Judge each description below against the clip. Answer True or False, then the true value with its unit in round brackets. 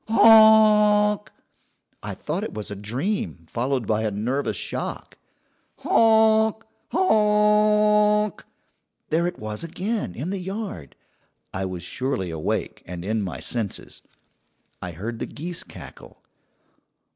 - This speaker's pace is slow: True (120 wpm)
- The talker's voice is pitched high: False (175 Hz)